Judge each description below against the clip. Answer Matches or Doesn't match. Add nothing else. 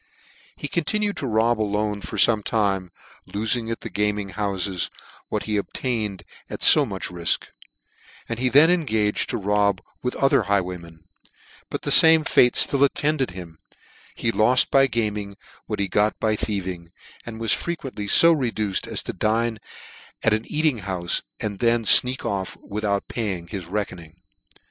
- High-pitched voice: Doesn't match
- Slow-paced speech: Doesn't match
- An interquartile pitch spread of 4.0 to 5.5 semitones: Doesn't match